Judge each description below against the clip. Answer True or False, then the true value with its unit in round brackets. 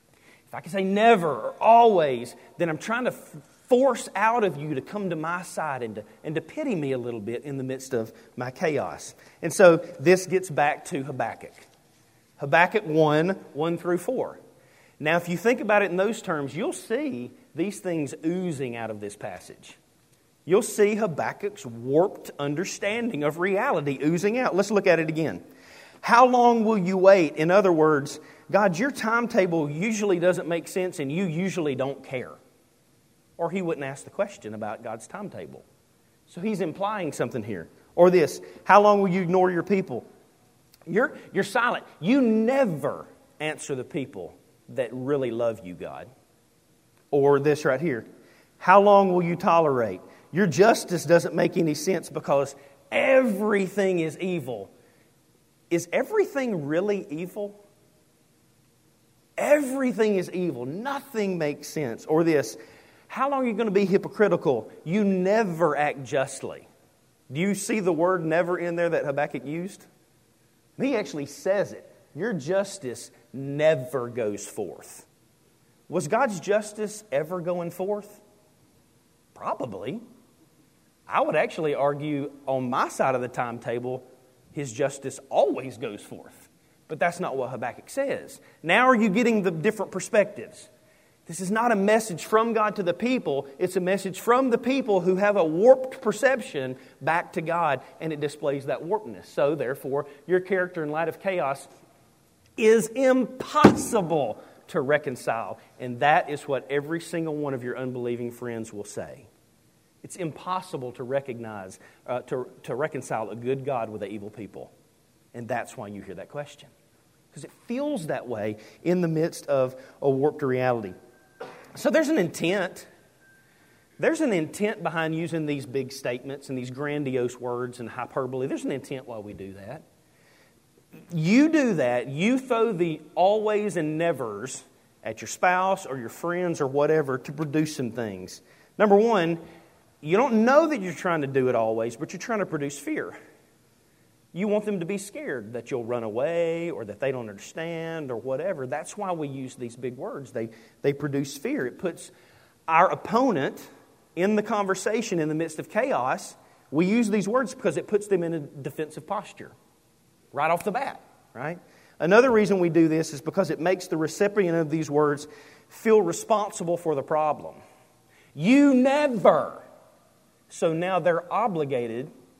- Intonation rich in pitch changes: True (6.5 semitones)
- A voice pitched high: False (165 Hz)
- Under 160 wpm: False (165 wpm)